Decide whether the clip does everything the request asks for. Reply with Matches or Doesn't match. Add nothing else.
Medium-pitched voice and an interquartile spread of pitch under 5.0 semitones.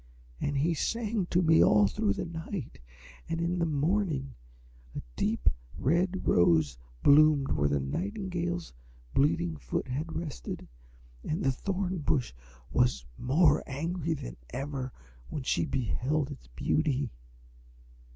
Doesn't match